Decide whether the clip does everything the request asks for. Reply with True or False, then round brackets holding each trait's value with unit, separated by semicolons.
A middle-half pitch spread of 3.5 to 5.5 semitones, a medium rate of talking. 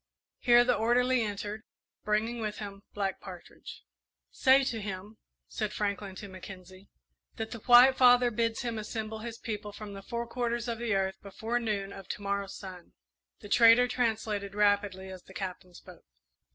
False (3.0 semitones; 165 wpm)